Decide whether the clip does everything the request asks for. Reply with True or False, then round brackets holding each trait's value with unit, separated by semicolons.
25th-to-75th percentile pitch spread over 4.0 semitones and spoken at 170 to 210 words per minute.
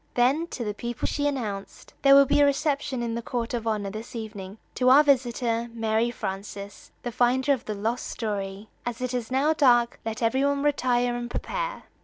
False (3.4 semitones; 200 wpm)